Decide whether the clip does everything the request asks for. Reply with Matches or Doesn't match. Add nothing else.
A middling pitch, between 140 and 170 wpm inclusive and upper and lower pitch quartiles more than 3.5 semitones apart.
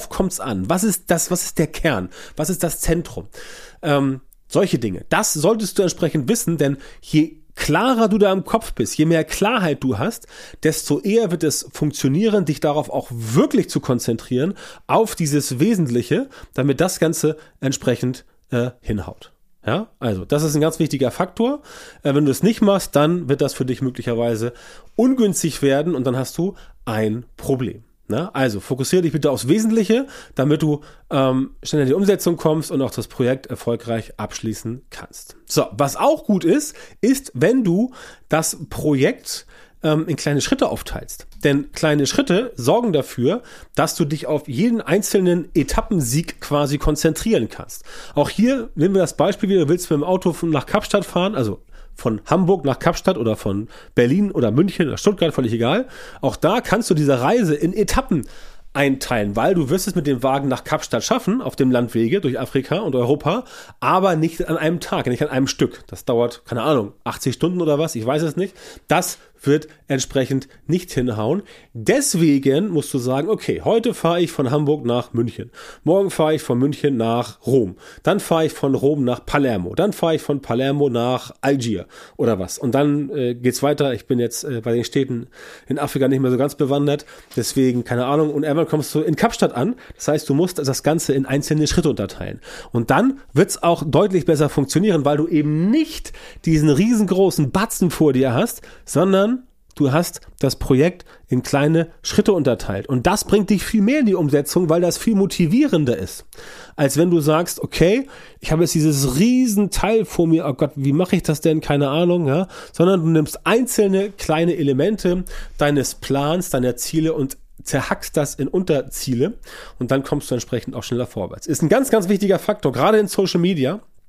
Doesn't match